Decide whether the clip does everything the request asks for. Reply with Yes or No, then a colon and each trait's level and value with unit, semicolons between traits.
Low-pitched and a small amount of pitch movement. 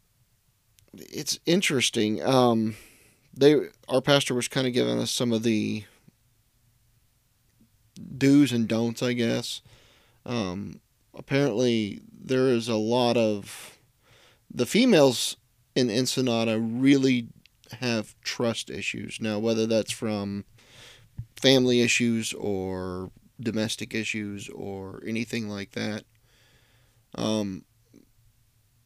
Yes: low, 115 Hz; narrow, 2.1 semitones